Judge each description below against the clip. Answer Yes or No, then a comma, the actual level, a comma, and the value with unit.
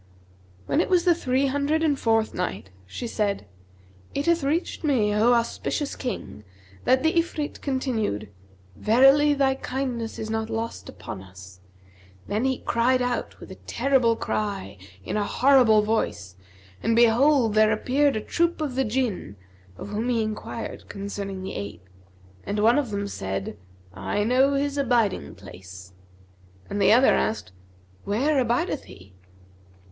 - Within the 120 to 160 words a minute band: Yes, average, 150 wpm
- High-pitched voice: Yes, high, 230 Hz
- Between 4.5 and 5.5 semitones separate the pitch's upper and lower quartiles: Yes, average, 5.0 semitones